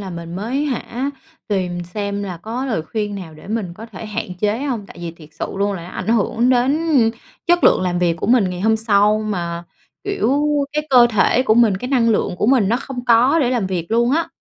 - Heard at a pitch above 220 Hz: No, high, 215 Hz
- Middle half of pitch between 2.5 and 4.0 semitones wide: No, average, 5.0 semitones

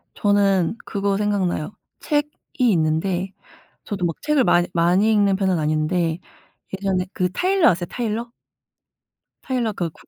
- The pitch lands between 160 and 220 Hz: Yes, high, 195 Hz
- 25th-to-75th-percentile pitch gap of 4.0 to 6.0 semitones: No, average, 3.3 semitones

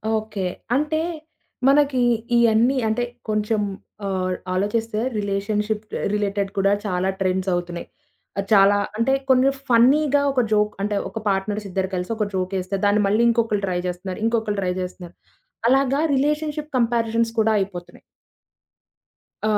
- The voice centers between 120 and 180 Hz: No, high, 210 Hz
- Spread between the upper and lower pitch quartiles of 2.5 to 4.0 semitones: Yes, average, 3.4 semitones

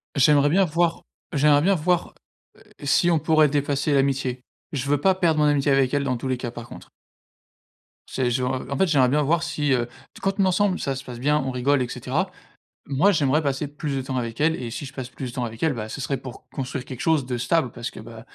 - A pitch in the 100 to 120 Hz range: No, medium, 140 Hz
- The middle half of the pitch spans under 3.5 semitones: Yes, average, 3.0 semitones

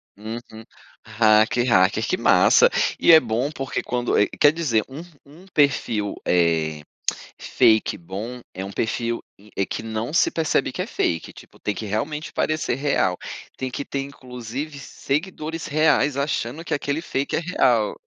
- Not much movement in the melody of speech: No, average, 5.2 semitones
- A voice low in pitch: Yes, low, 125 Hz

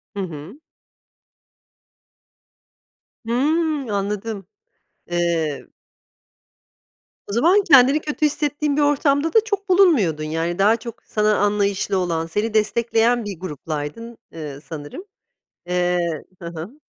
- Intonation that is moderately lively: No, wide, 8.6 semitones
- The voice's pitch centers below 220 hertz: Yes, high, 210 Hz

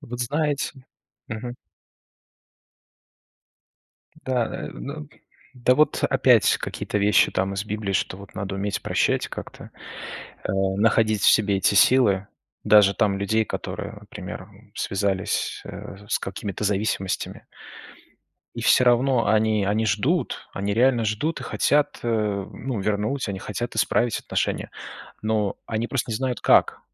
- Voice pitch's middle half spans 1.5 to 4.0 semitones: Yes, average, 3.4 semitones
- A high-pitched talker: No, low, 110 Hz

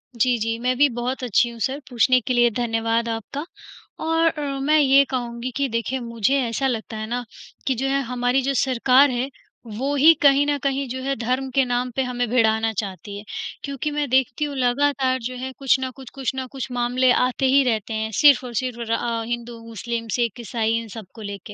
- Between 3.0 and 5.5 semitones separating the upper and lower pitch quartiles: No, narrow, 2.6 semitones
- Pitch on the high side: Yes, very high, 250 Hz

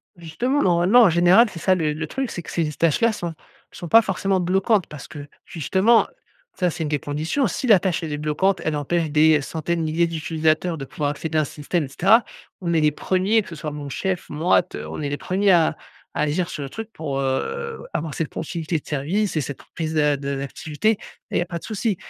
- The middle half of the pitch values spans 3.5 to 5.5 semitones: Yes, average, 3.9 semitones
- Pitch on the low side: No, medium, 165 Hz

